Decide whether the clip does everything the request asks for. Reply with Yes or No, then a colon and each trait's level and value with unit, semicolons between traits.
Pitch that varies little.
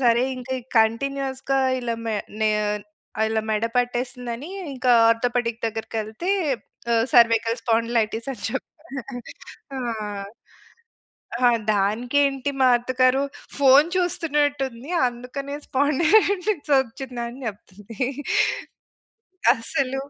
No: average, 3.2 semitones